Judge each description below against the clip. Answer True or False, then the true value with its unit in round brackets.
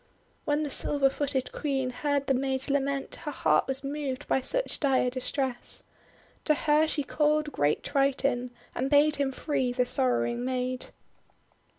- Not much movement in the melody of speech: True (2.3 semitones)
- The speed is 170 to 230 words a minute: False (155 wpm)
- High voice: True (275 Hz)